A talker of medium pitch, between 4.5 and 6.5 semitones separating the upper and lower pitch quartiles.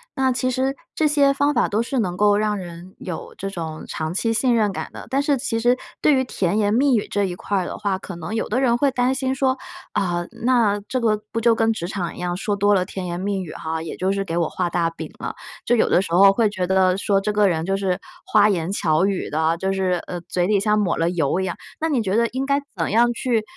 No: high, 205 Hz; average, 4.8 semitones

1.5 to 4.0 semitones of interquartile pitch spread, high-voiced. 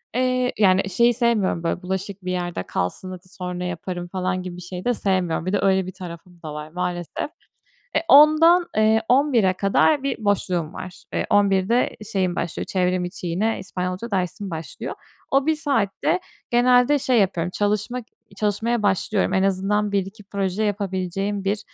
Yes: average, 3.5 semitones; high, 195 Hz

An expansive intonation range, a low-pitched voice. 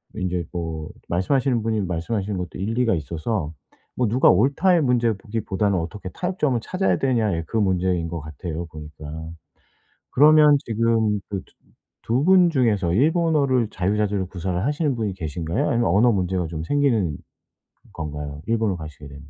Yes: wide, 6.3 semitones; low, 105 Hz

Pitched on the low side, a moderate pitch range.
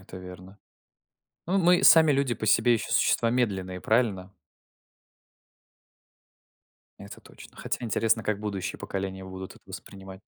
Yes: low, 100 Hz; average, 4.0 semitones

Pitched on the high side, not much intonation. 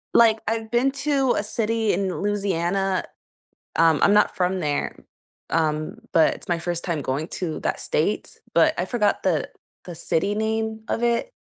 No: high, 195 Hz; average, 4.8 semitones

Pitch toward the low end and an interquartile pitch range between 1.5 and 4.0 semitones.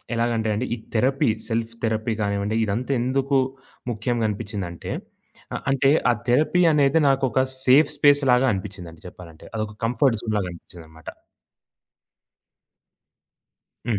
No: low, 115 Hz; average, 4.6 semitones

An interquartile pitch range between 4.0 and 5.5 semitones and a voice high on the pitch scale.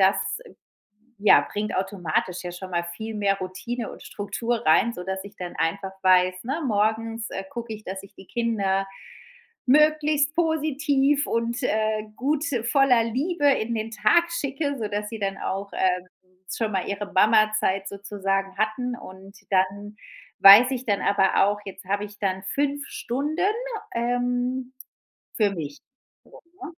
Yes: average, 4.3 semitones; high, 215 Hz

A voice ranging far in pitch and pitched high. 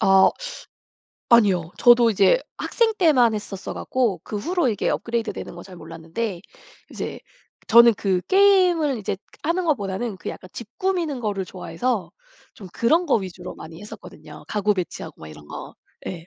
Yes: wide, 5.8 semitones; high, 215 Hz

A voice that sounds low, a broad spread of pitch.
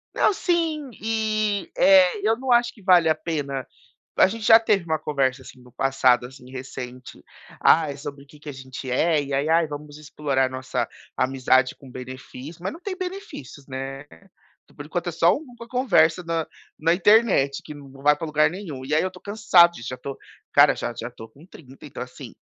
No: medium, 150 Hz; wide, 6.7 semitones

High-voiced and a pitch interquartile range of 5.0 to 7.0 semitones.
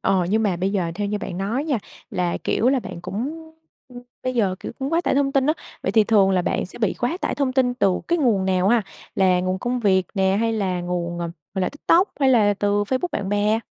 Yes: high, 205 Hz; average, 5.3 semitones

